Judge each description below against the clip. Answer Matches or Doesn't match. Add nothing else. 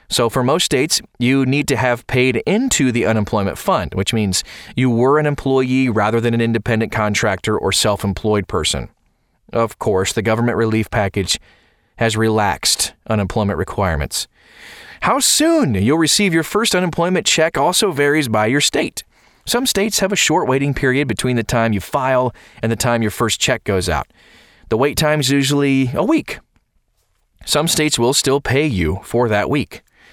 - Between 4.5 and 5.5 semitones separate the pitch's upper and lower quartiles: Matches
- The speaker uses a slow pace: Doesn't match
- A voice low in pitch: Matches